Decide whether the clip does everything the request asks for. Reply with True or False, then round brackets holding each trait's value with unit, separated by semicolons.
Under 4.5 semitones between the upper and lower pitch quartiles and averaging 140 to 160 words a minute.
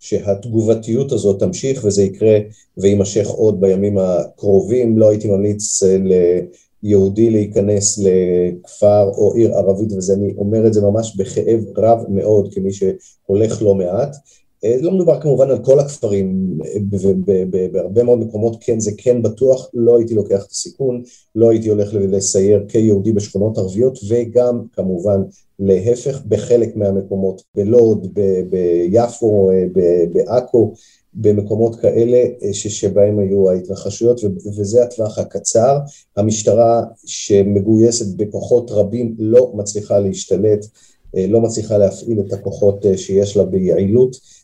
False (2.8 semitones; 125 wpm)